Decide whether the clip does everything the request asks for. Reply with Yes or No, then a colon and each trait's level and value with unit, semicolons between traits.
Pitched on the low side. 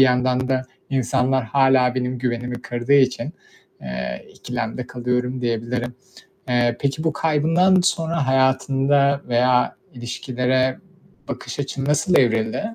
Yes: low, 130 Hz